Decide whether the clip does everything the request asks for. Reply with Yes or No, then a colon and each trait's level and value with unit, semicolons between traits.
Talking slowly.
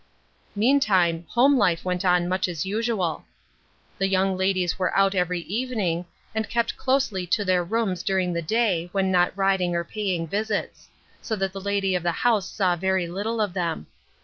No: average, 175 wpm